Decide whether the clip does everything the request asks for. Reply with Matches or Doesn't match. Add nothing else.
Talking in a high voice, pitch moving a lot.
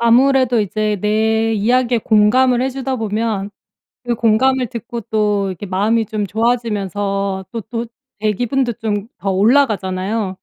Doesn't match